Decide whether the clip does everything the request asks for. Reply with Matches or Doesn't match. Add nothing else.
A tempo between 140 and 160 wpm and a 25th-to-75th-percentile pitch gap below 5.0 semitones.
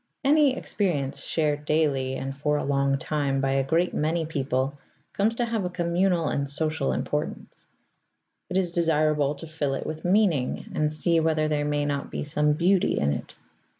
Doesn't match